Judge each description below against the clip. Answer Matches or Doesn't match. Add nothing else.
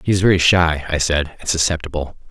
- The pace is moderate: Doesn't match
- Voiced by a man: Matches